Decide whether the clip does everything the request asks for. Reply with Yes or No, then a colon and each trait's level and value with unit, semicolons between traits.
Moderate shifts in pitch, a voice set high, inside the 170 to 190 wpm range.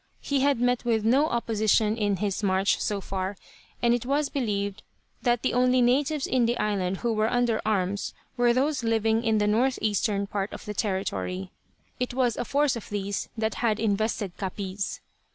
Yes: average, 3.3 semitones; high, 220 Hz; average, 180 wpm